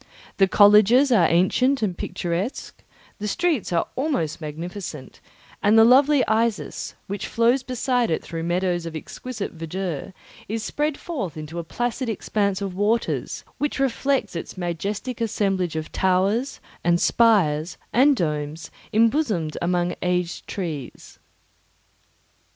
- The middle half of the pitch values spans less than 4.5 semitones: No, wide, 5.6 semitones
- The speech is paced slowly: Yes, slow, 130 wpm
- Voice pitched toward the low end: No, high, 200 Hz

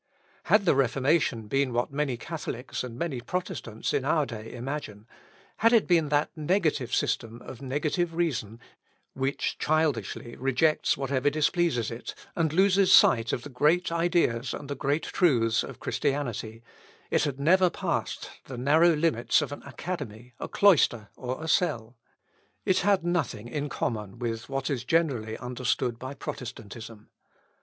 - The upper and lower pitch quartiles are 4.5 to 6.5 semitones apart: Yes, average, 5.3 semitones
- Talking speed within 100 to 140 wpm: No, average, 150 wpm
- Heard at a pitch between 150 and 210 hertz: No, low, 135 Hz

